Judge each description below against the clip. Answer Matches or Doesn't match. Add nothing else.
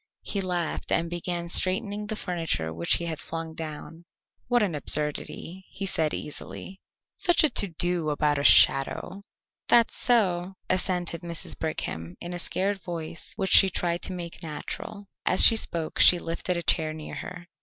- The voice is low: Doesn't match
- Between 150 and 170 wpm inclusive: Matches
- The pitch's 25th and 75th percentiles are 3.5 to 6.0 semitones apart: Doesn't match